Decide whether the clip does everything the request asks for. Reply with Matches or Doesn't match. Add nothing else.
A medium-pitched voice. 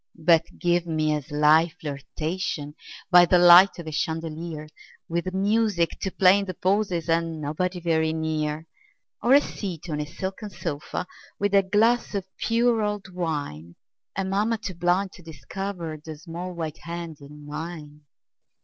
Matches